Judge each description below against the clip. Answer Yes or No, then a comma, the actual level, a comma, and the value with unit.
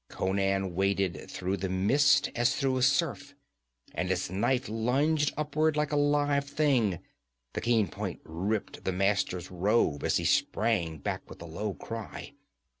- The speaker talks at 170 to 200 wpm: No, average, 155 wpm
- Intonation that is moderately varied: No, wide, 7.0 semitones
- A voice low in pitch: Yes, low, 110 Hz